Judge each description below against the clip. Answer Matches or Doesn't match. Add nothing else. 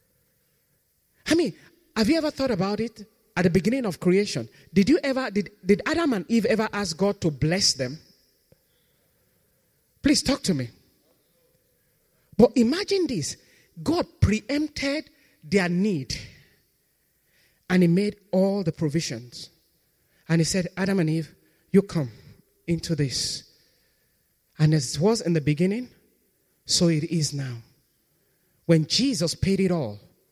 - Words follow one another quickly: Doesn't match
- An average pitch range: Doesn't match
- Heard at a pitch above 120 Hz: Matches